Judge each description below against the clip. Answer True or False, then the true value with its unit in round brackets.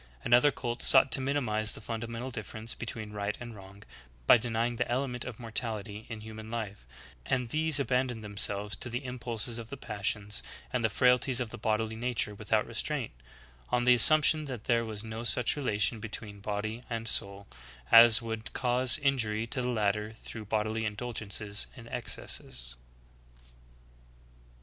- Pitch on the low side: True (115 Hz)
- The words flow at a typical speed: True (160 wpm)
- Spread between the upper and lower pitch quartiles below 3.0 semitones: True (2.5 semitones)